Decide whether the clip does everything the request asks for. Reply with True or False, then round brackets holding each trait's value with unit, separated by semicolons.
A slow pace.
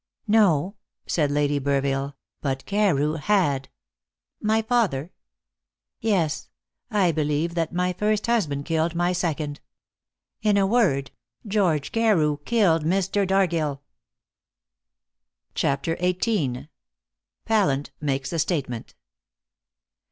True (100 wpm)